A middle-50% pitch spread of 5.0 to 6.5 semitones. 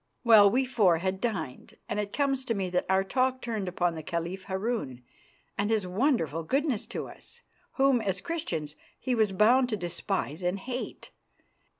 Yes: wide, 5.5 semitones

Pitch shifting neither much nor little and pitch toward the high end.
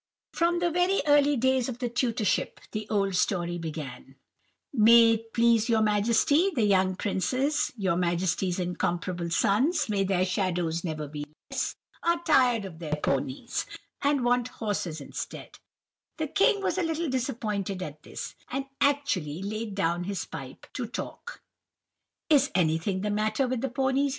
No: wide, 6.7 semitones; high, 215 Hz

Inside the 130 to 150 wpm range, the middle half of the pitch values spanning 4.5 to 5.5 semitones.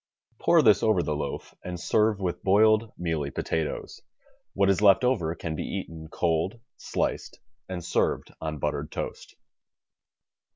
Yes: average, 140 wpm; average, 4.8 semitones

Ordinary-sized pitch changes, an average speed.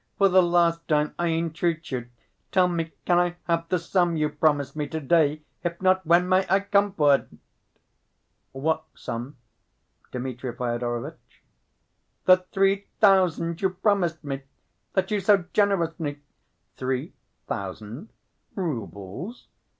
No: average, 4.3 semitones; slow, 130 wpm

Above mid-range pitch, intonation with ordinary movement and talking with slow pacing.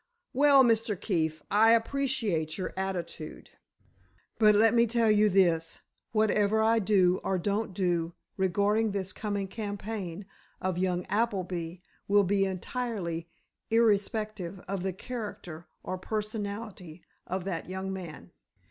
Yes: high, 200 Hz; average, 3.3 semitones; slow, 125 wpm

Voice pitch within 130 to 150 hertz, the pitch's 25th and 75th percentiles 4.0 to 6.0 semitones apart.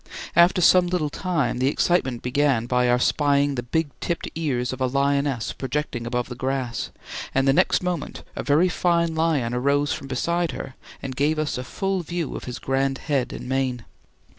Yes: medium, 140 Hz; average, 4.3 semitones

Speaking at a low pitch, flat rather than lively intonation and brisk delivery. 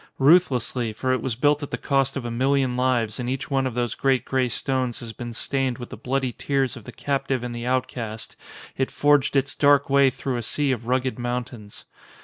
Yes: low, 130 Hz; narrow, 2.0 semitones; fast, 215 wpm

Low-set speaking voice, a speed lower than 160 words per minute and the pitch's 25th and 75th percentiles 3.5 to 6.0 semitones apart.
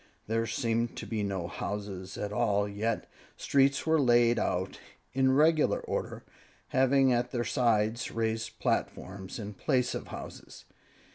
Yes: low, 115 Hz; average, 140 wpm; average, 3.9 semitones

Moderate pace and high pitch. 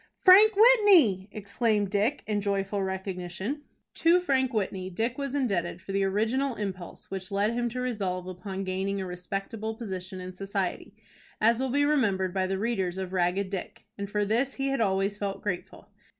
Yes: average, 175 wpm; high, 200 Hz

